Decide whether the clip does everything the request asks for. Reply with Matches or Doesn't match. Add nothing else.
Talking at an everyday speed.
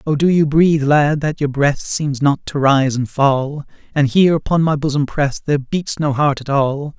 Doesn't match